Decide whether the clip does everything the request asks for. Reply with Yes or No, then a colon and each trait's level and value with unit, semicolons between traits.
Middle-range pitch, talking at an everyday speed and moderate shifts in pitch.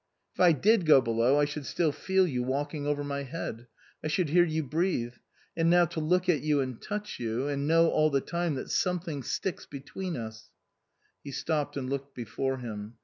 No: medium, 145 Hz; fast, 210 wpm; average, 4.2 semitones